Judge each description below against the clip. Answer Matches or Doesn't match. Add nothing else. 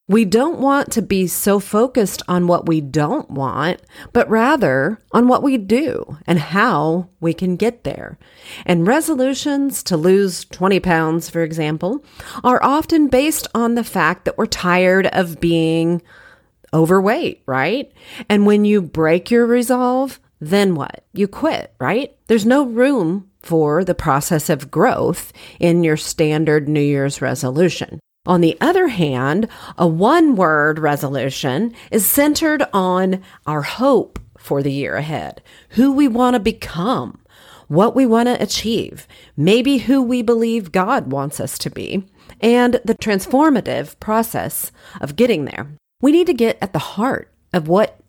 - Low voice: Doesn't match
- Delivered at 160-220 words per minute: Doesn't match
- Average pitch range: Doesn't match